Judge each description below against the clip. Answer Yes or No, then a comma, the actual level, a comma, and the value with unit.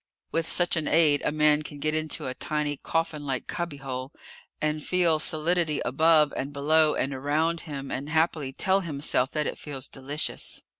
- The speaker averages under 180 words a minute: Yes, average, 165 wpm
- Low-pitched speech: No, medium, 150 Hz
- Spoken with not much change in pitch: Yes, narrow, 2.2 semitones